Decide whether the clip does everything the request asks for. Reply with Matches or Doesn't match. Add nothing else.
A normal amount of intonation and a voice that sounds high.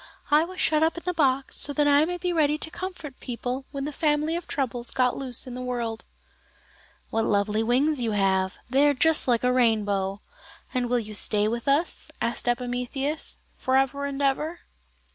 Matches